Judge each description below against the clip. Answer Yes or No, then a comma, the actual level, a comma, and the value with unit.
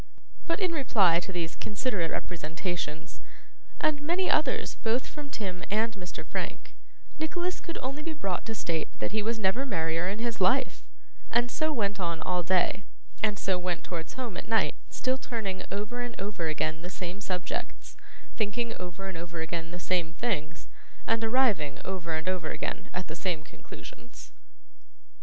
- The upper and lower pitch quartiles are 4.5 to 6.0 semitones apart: Yes, wide, 5.6 semitones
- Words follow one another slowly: No, average, 170 wpm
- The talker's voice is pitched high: Yes, high, 195 Hz